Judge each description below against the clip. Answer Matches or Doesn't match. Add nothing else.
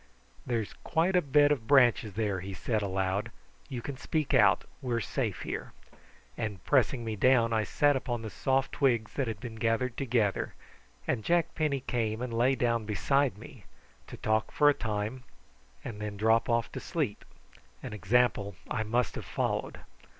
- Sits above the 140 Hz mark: Doesn't match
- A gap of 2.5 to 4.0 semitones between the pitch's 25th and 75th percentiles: Matches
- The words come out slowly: Doesn't match